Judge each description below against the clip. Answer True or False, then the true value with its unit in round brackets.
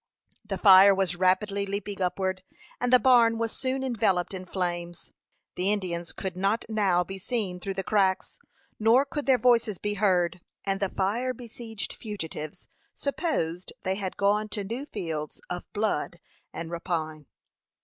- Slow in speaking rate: False (155 wpm)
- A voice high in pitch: True (195 Hz)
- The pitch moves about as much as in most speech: True (3.6 semitones)